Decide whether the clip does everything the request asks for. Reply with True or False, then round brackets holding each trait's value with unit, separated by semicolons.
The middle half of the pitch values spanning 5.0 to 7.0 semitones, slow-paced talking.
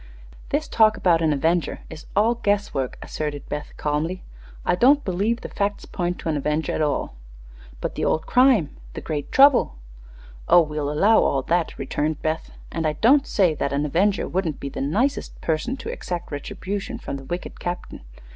False (5.6 semitones; 185 wpm)